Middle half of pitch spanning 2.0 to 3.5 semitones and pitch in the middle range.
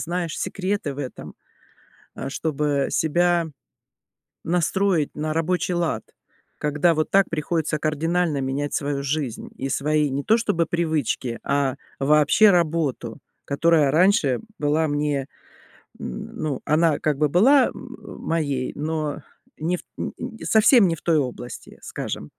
Yes: average, 3.2 semitones; medium, 155 Hz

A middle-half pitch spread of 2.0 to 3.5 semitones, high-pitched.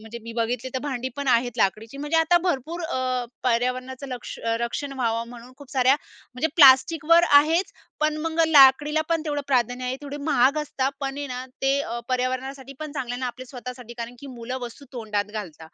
Yes: average, 3.0 semitones; very high, 260 Hz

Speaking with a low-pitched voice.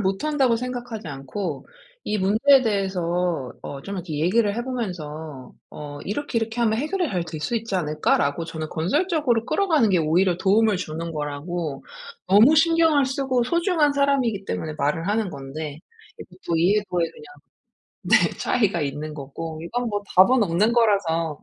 No: high, 195 Hz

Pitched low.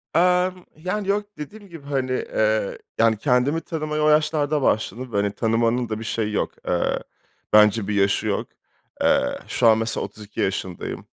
Yes: low, 125 Hz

